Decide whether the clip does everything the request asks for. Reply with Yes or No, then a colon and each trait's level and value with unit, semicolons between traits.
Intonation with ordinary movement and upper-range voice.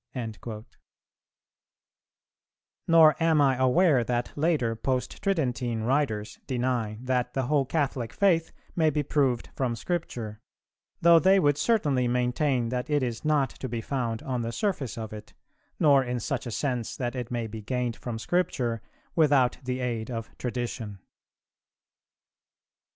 No: average, 3.8 semitones; low, 125 Hz